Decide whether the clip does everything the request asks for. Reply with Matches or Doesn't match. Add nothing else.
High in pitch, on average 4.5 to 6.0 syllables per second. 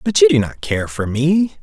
Doesn't match